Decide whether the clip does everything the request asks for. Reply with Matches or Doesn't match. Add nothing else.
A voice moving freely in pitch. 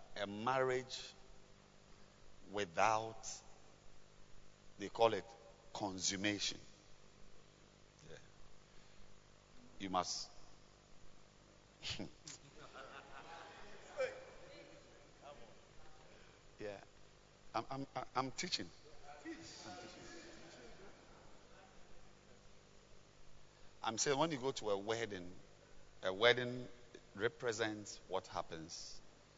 Doesn't match